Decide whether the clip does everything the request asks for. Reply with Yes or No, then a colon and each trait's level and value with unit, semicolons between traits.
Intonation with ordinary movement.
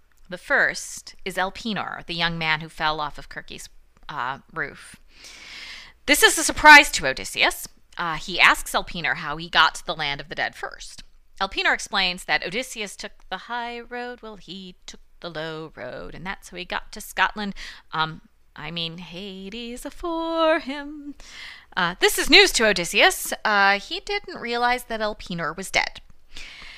No: wide, 8.1 semitones